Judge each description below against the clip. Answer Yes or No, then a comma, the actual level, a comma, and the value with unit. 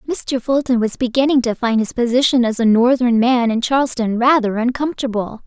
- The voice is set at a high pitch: Yes, high, 245 Hz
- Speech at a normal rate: Yes, average, 175 wpm